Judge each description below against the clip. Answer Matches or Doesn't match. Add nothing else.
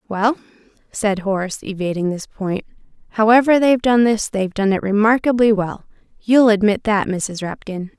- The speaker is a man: Doesn't match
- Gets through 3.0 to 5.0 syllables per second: Doesn't match